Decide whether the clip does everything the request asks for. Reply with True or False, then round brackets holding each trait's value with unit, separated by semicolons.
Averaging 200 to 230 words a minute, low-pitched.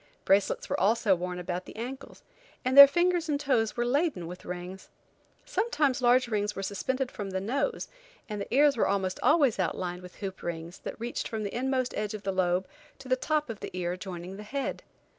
False (205 wpm; 215 Hz)